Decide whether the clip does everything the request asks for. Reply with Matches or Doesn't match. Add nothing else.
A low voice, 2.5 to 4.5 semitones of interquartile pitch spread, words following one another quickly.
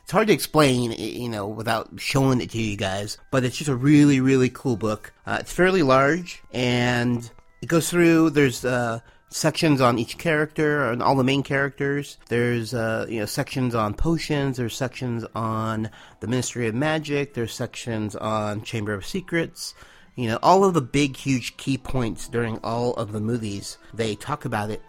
Doesn't match